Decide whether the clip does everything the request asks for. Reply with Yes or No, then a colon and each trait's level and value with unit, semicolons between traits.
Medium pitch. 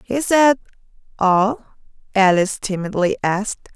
No: high, 215 Hz